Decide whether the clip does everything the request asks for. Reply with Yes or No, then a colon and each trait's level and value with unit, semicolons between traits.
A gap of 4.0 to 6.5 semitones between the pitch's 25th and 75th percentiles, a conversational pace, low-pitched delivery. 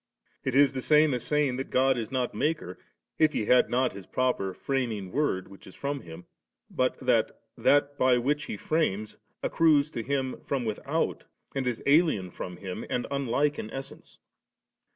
Yes: average, 4.5 semitones; average, 175 wpm; low, 130 Hz